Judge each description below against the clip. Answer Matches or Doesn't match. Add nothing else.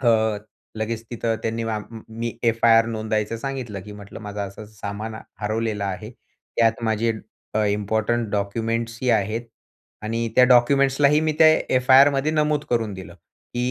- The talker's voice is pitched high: Doesn't match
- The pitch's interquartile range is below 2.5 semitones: Matches